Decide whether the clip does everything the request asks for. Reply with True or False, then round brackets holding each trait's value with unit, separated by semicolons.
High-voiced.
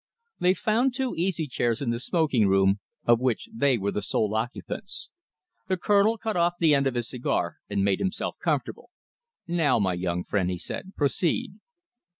False (135 Hz)